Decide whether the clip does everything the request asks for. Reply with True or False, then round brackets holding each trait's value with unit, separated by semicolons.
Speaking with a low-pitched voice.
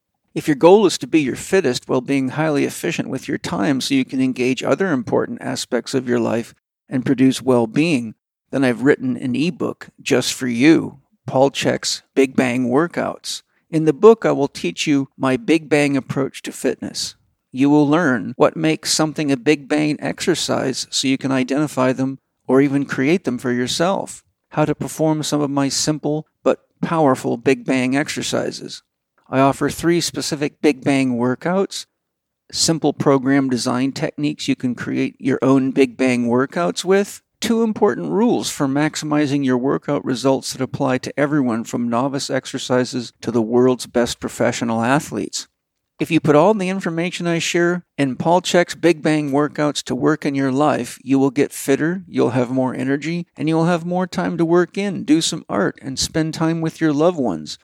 False (145 Hz)